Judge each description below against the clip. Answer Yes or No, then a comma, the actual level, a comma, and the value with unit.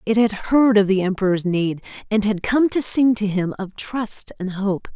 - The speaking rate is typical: No, fast, 220 wpm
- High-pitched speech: Yes, high, 210 Hz